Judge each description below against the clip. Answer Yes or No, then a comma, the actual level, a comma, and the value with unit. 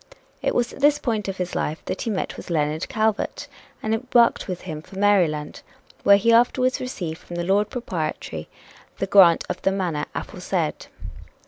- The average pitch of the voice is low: No, high, 195 Hz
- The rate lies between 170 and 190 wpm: Yes, average, 180 wpm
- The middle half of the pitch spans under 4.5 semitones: No, average, 5.0 semitones